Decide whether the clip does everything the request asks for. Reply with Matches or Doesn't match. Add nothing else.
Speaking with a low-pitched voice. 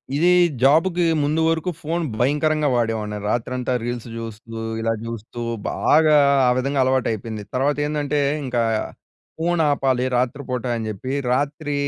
Matches